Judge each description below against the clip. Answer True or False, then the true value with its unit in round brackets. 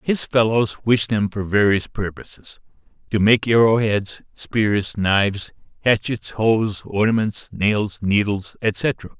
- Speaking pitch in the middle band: False (105 Hz)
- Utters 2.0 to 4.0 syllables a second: True (3.7 syllables/s)